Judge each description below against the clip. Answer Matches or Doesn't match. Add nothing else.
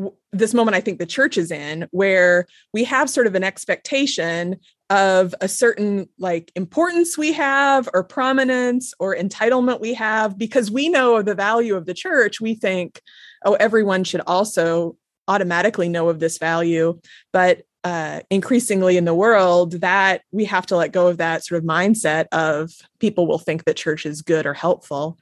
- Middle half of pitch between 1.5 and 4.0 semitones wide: Doesn't match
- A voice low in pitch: Doesn't match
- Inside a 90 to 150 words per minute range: Doesn't match